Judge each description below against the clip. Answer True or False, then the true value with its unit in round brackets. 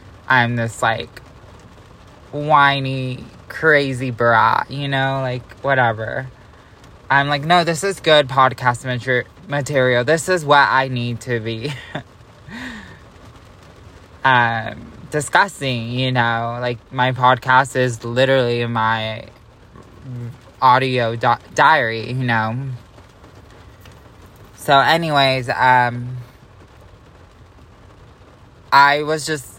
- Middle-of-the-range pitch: False (125 Hz)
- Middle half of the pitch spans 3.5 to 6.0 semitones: False (3.0 semitones)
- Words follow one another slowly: True (95 wpm)